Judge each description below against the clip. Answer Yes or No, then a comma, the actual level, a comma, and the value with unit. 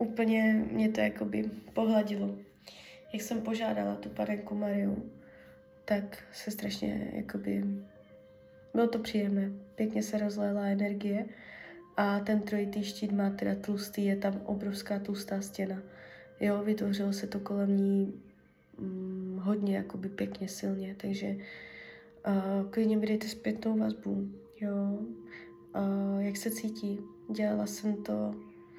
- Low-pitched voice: No, high, 200 Hz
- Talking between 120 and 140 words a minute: Yes, average, 125 wpm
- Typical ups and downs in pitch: No, narrow, 2.3 semitones